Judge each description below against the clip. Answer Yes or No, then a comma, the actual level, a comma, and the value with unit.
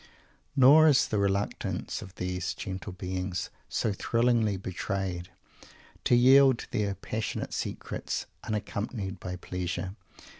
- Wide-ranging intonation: No, average, 4.1 semitones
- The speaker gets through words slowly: Yes, slow, 110 wpm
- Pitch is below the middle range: Yes, low, 100 Hz